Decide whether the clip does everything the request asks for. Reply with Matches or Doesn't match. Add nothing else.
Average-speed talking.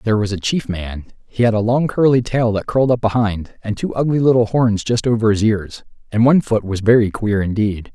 Doesn't match